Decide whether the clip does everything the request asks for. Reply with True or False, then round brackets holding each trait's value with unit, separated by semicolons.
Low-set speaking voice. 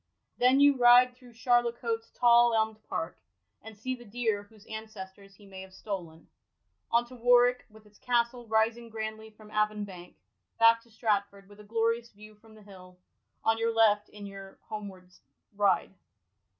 False (220 Hz)